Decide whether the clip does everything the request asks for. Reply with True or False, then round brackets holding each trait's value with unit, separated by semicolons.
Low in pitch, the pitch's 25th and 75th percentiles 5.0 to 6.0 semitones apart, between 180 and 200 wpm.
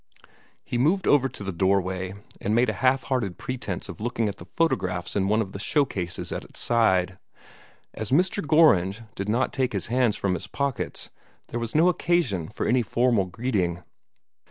True (110 Hz; 5.4 semitones; 190 wpm)